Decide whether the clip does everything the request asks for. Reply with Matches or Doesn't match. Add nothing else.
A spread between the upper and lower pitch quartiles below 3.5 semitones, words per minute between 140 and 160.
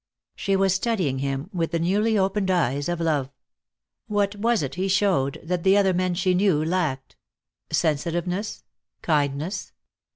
Doesn't match